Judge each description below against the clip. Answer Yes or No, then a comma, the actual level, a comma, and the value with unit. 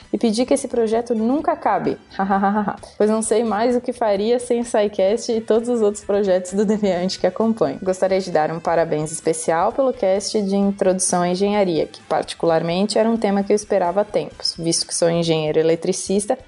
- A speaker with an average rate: No, fast, 195 wpm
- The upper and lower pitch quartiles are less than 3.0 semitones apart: No, average, 3.6 semitones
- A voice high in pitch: Yes, high, 200 Hz